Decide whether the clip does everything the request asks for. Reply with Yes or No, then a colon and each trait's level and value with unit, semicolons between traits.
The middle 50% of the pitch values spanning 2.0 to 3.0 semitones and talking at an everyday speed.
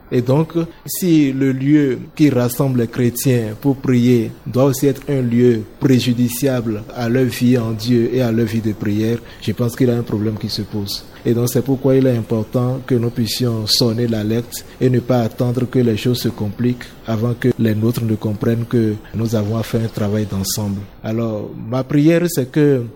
Yes: narrow, 2.5 semitones; average, 205 wpm